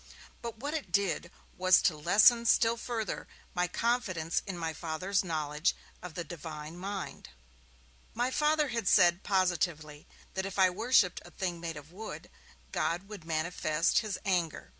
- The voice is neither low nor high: Yes, medium, 180 Hz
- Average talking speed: Yes, average, 155 wpm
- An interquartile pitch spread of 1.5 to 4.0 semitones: No, average, 4.5 semitones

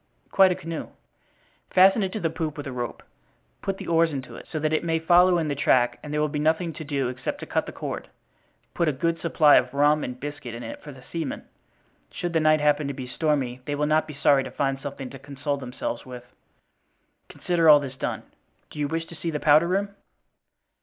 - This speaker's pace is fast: Yes, fast, 230 wpm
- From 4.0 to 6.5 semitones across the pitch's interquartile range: No, average, 3.1 semitones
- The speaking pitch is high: No, medium, 150 Hz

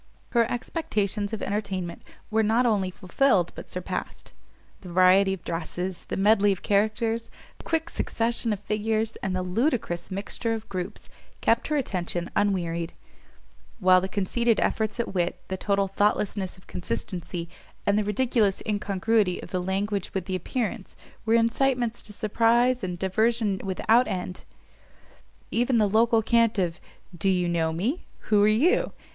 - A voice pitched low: No, high, 205 Hz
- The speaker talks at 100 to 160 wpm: Yes, average, 150 wpm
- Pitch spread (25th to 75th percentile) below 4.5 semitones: Yes, average, 3.6 semitones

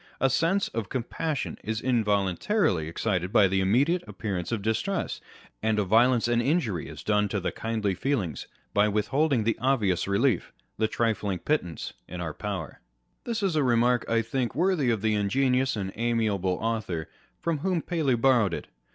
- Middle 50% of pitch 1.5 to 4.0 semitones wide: No, average, 5.1 semitones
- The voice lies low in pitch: Yes, low, 115 Hz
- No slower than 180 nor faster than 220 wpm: No, average, 170 wpm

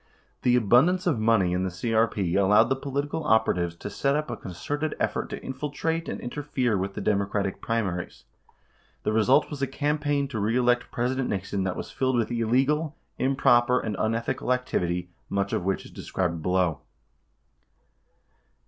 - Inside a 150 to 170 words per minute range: Yes, average, 160 wpm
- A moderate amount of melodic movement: No, wide, 5.7 semitones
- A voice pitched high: No, low, 115 Hz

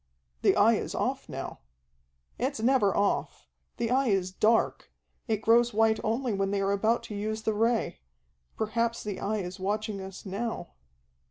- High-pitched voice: Yes, high, 215 Hz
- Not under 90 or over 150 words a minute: No, average, 165 wpm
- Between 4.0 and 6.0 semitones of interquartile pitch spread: No, narrow, 2.5 semitones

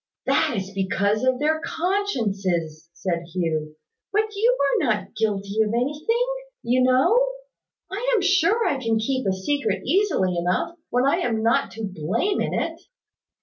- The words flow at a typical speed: Yes, average, 155 wpm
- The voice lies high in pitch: Yes, high, 235 Hz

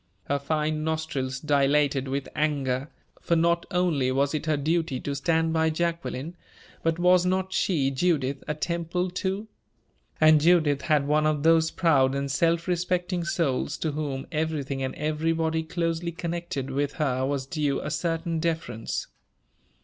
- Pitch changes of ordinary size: Yes, average, 3.2 semitones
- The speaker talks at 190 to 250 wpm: No, average, 150 wpm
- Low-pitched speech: No, medium, 155 Hz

